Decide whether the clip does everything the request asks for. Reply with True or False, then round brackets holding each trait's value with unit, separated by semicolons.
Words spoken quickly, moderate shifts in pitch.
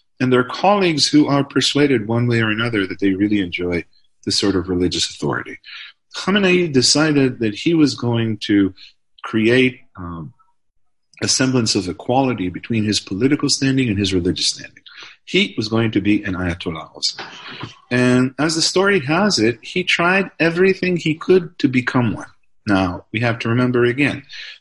False (165 wpm; 6.5 semitones)